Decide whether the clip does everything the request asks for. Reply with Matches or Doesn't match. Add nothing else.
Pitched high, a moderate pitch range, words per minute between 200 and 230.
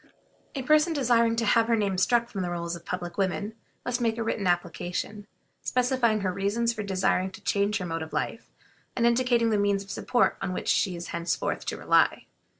Matches